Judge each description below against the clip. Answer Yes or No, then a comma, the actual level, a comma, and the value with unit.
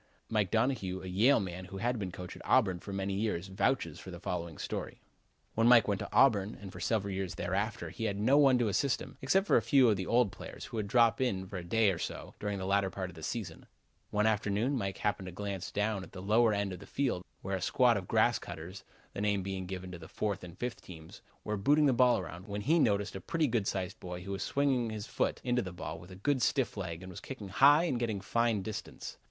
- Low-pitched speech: Yes, low, 100 Hz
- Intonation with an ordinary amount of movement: Yes, average, 4.0 semitones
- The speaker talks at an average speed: No, fast, 250 wpm